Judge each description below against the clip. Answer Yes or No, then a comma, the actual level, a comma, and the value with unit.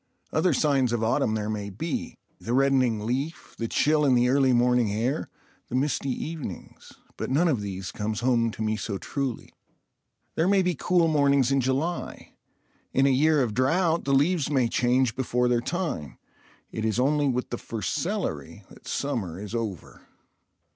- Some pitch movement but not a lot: Yes, average, 4.2 semitones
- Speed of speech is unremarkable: Yes, average, 170 wpm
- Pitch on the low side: Yes, low, 130 Hz